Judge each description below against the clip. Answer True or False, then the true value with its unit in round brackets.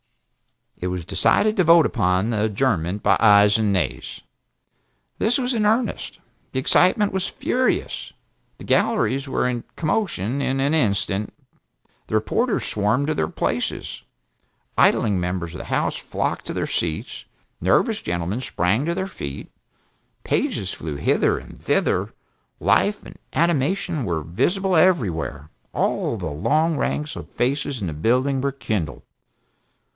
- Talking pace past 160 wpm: False (140 wpm)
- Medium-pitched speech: False (120 Hz)